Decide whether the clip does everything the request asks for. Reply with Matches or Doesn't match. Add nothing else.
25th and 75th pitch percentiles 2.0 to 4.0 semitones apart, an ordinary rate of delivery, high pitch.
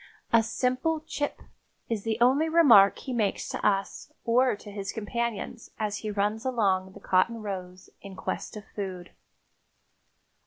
Matches